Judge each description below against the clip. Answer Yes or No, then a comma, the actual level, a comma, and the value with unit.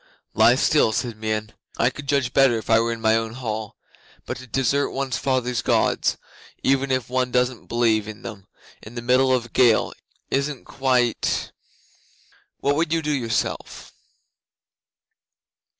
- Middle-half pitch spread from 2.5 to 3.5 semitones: Yes, average, 2.9 semitones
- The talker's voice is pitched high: No, low, 125 Hz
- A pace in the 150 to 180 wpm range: Yes, average, 155 wpm